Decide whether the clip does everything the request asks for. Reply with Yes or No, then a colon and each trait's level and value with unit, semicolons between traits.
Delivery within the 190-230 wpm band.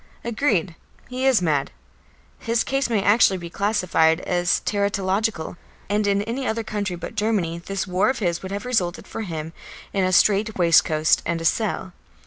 No: average, 170 wpm